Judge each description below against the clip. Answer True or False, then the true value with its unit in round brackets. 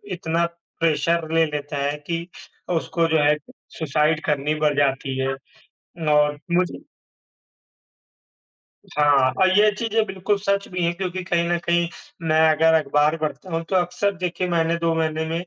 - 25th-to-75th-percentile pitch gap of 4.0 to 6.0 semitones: False (2.7 semitones)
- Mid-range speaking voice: True (165 Hz)